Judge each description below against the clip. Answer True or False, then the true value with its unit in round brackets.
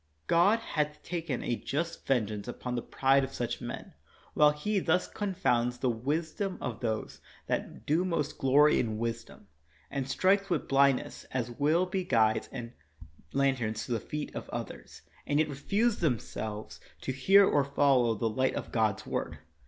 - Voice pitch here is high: False (135 Hz)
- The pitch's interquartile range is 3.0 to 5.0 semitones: False (5.6 semitones)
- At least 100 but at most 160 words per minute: False (170 wpm)